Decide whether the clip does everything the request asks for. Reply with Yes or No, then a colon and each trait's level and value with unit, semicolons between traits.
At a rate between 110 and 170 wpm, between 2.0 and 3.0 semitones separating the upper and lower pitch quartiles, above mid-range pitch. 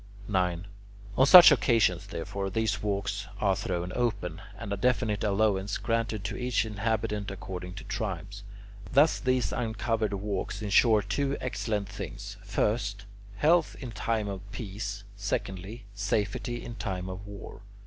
No: average, 140 wpm; narrow, 2.5 semitones; low, 105 Hz